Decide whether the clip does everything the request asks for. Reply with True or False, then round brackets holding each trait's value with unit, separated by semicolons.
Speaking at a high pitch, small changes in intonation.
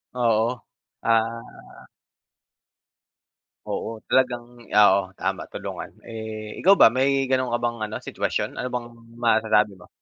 False (115 Hz; 2.3 semitones)